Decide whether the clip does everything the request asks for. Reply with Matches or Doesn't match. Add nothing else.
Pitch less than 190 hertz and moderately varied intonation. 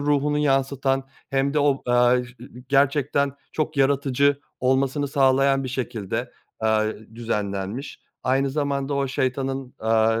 Doesn't match